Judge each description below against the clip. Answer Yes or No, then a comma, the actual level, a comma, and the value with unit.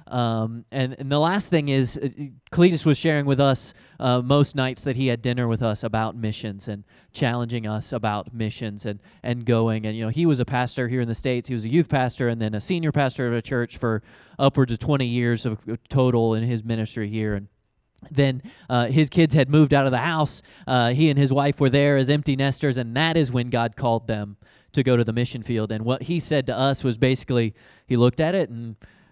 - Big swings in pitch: No, average, 3.4 semitones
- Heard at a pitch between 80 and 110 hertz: No, low, 125 Hz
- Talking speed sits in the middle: No, fast, 235 wpm